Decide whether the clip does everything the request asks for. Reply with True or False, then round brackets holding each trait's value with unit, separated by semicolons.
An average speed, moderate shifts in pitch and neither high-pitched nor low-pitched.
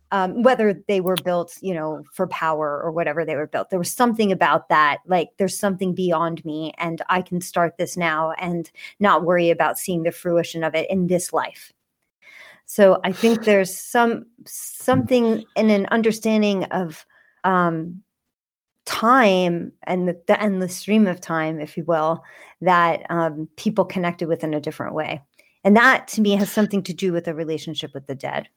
True (185 wpm; 3.5 semitones; 180 Hz)